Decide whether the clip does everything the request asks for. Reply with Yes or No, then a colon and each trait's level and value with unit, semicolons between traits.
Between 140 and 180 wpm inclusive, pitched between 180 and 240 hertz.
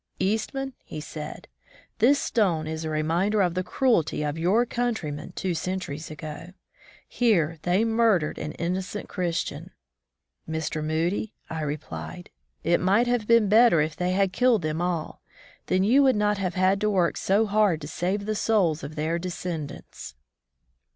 Yes: average, 160 wpm; medium, 185 Hz